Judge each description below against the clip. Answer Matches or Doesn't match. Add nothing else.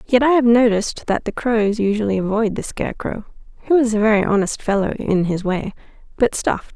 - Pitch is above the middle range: Matches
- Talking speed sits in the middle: Matches